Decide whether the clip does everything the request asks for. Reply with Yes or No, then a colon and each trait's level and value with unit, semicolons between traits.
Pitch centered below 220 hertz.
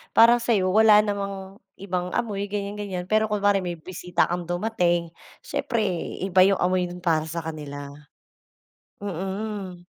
Yes: high, 190 Hz